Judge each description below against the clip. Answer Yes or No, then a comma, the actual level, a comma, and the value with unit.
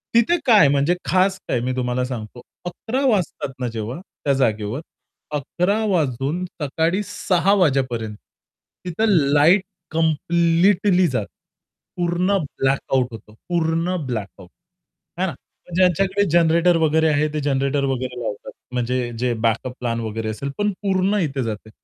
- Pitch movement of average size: No, wide, 6.3 semitones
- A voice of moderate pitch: Yes, medium, 150 Hz